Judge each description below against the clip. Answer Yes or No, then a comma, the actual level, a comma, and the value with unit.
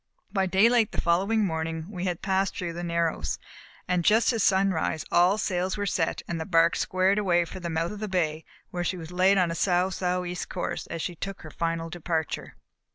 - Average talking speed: No, fast, 215 wpm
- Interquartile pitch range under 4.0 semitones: Yes, narrow, 2.4 semitones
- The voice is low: No, medium, 180 Hz